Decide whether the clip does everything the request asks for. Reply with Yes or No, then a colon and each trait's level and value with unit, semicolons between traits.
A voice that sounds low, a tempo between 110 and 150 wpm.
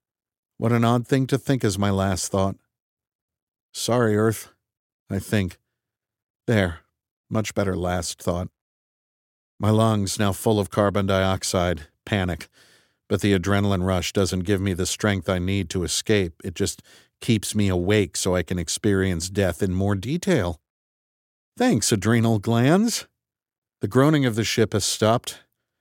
Yes: low, 100 Hz; average, 145 wpm